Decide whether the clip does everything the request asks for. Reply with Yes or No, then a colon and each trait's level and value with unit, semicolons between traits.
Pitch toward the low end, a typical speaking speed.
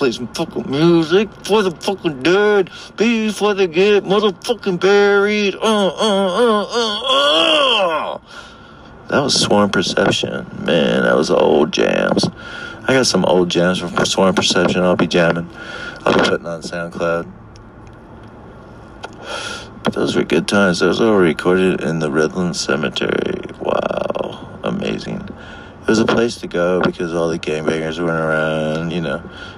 Yes: low, 115 Hz; average, 145 wpm